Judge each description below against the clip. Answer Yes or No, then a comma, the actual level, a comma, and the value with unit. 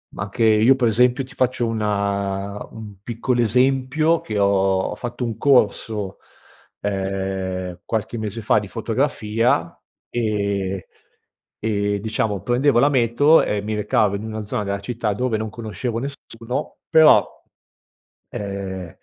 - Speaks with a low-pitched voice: Yes, low, 110 Hz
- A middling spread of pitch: Yes, average, 3.3 semitones